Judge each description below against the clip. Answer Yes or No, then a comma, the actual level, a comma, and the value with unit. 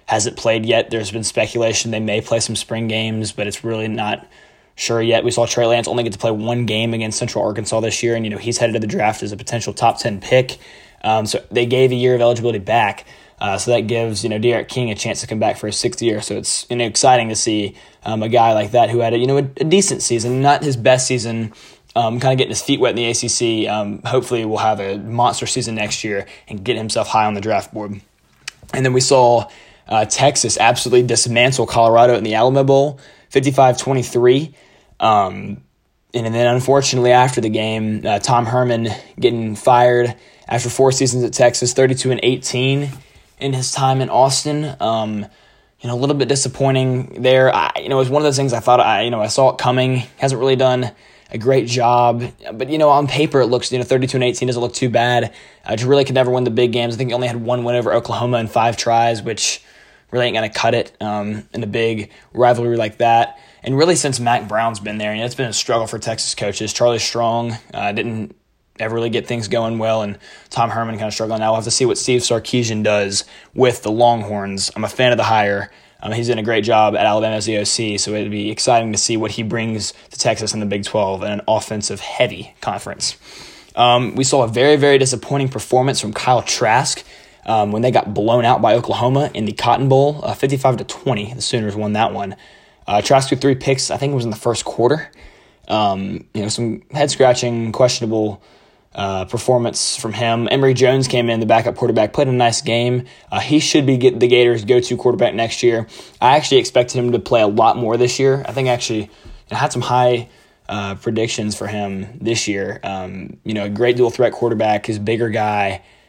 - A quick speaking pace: Yes, fast, 230 wpm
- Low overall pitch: Yes, low, 120 Hz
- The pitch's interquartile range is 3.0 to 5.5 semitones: No, narrow, 2.5 semitones